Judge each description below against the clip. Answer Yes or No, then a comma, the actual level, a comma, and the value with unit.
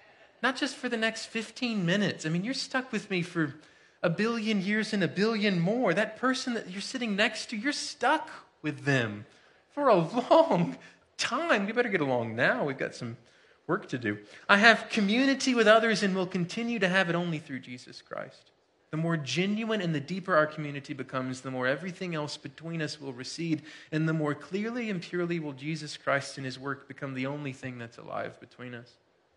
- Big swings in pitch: Yes, wide, 7.6 semitones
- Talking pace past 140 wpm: Yes, average, 200 wpm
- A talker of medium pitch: Yes, medium, 180 Hz